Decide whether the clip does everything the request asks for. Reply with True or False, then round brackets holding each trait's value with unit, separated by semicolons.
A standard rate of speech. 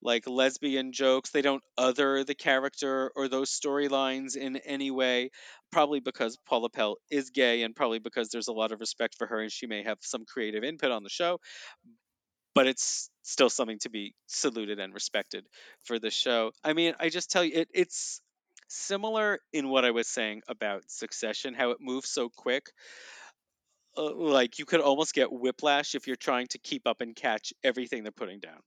True (195 wpm)